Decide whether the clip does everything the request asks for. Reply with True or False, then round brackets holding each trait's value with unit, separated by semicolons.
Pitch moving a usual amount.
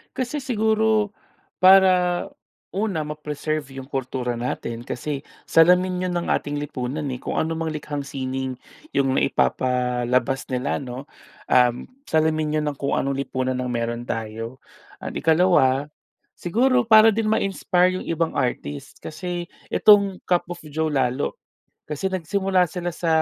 False (5.8 semitones)